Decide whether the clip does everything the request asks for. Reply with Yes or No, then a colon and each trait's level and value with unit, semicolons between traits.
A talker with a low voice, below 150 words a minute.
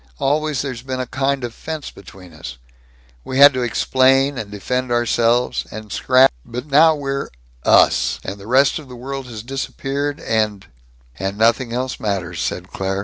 No: low, 125 Hz; average, 175 wpm